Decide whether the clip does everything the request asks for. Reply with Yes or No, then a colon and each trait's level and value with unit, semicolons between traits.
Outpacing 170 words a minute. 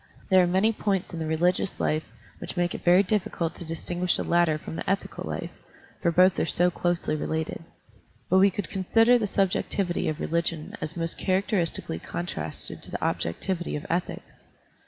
Yes: average, 180 wpm